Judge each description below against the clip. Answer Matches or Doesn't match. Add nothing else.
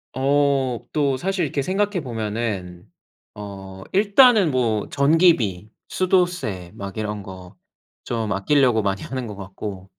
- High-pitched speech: Doesn't match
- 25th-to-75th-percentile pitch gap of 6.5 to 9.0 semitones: Matches